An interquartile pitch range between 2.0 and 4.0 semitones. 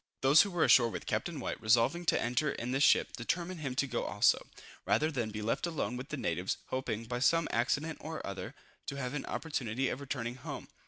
No: average, 4.5 semitones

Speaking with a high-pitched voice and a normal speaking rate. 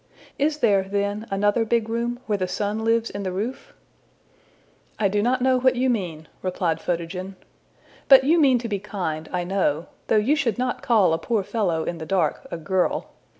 Yes: high, 205 Hz; average, 195 wpm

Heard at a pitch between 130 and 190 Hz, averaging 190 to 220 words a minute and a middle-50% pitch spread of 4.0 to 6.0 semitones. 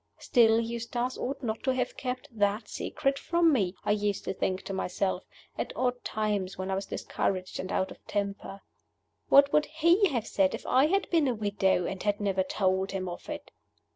No: high, 215 Hz; average, 200 wpm; average, 5.1 semitones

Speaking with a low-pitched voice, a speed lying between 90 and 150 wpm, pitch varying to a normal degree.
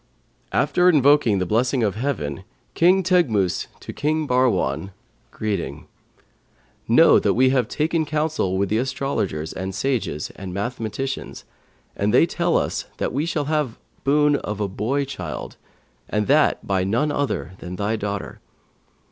No: low, 125 Hz; average, 145 wpm; wide, 6.8 semitones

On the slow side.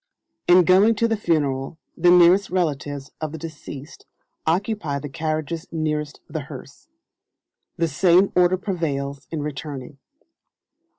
Yes: slow, 125 wpm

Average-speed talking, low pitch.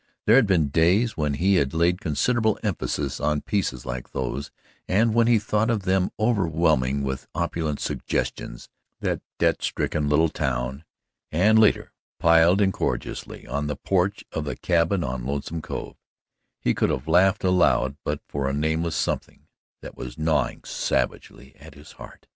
Yes: average, 160 wpm; very low, 80 Hz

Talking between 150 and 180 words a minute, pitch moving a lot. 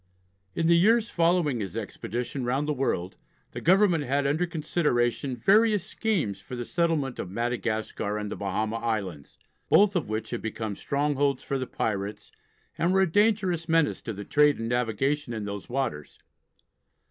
Yes: average, 165 wpm; wide, 7.1 semitones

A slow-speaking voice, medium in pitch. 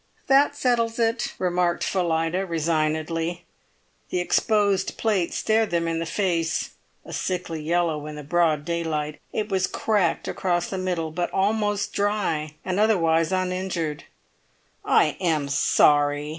Yes: slow, 130 wpm; medium, 175 Hz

